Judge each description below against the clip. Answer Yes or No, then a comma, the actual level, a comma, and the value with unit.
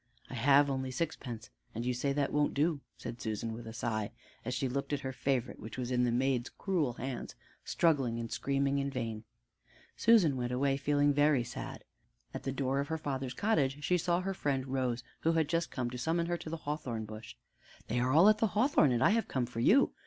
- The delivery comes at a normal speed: No, fast, 220 wpm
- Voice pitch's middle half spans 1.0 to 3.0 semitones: No, average, 3.9 semitones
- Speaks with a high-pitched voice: No, low, 135 Hz